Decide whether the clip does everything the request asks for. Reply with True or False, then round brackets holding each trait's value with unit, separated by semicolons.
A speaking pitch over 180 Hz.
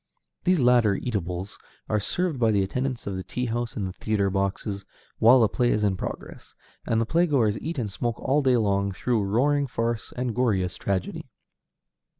False (115 Hz)